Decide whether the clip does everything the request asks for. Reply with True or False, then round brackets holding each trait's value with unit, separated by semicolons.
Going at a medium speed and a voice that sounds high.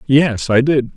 False (190 wpm; 135 Hz)